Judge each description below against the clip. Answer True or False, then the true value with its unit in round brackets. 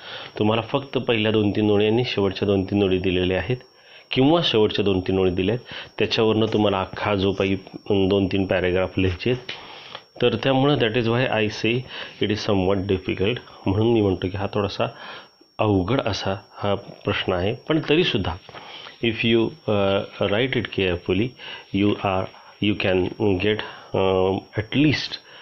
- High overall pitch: False (105 Hz)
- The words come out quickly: True (150 wpm)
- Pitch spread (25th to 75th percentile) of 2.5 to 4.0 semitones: True (3.4 semitones)